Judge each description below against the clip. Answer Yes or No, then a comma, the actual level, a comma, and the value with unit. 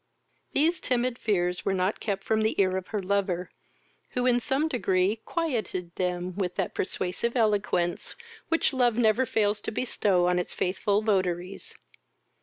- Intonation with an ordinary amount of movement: Yes, average, 4.5 semitones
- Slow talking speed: No, average, 155 wpm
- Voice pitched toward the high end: Yes, high, 205 Hz